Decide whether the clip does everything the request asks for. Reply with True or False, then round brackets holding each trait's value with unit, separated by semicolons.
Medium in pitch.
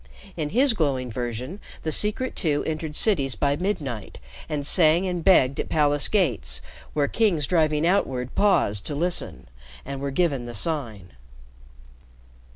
True (150 Hz)